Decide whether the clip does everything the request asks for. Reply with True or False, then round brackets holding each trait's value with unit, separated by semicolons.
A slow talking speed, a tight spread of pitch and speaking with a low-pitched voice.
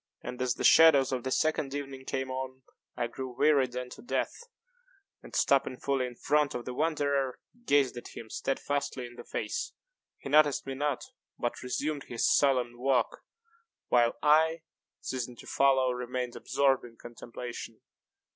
False (155 wpm; 2.3 semitones; 130 Hz)